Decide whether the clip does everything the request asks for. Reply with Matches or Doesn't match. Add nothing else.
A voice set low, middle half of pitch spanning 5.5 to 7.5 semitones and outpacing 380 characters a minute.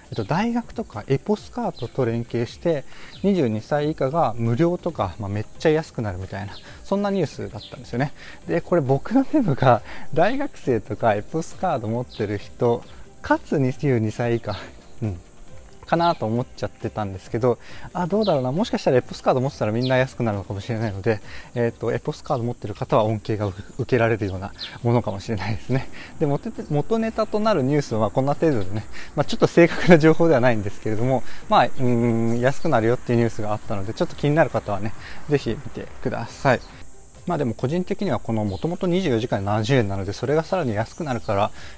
Matches